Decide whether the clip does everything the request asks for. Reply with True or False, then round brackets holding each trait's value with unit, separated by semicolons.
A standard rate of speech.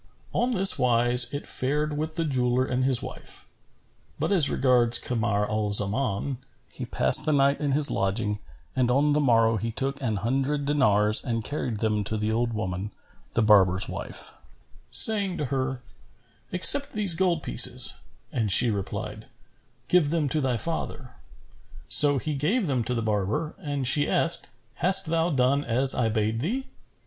True (165 wpm)